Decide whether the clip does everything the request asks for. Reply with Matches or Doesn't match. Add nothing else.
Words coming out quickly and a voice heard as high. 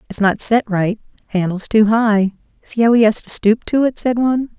Matches